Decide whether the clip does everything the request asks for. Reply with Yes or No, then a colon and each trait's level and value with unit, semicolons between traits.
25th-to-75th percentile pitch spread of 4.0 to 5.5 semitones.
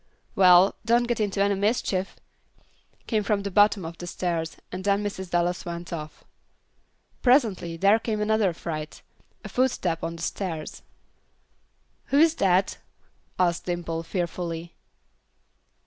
No: average, 3.4 semitones